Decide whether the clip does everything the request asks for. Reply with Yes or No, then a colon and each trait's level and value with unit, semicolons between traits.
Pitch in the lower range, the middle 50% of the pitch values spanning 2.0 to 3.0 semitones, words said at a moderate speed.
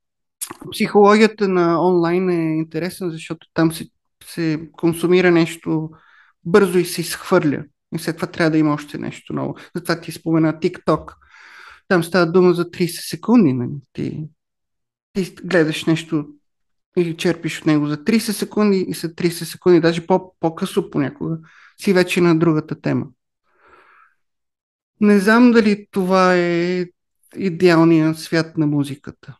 No: medium, 170 Hz; narrow, 2.5 semitones; average, 135 wpm